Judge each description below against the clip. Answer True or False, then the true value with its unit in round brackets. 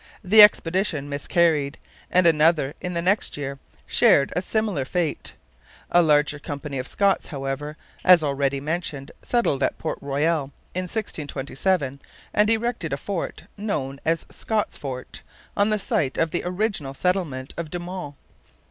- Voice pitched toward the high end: False (160 Hz)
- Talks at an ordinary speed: True (150 wpm)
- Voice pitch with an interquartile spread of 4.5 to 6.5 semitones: True (4.8 semitones)